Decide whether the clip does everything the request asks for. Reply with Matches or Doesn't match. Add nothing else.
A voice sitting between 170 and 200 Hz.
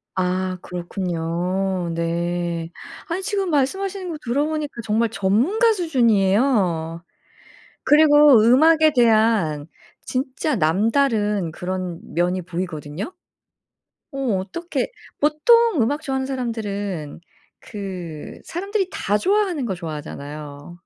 Doesn't match